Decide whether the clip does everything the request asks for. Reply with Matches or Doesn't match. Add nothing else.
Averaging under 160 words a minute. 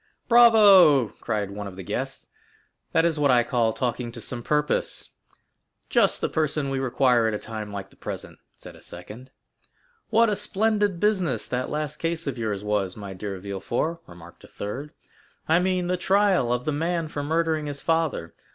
Doesn't match